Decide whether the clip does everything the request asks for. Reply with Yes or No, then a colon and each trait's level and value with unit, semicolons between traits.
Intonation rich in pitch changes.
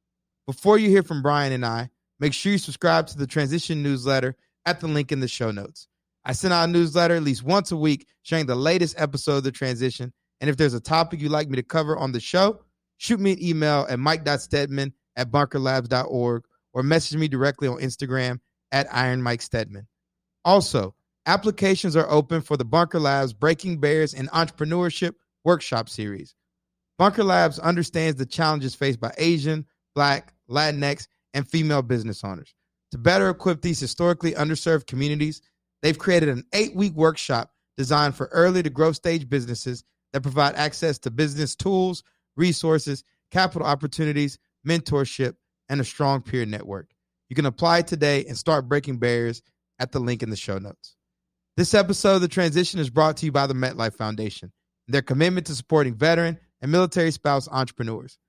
No: average, 4.1 semitones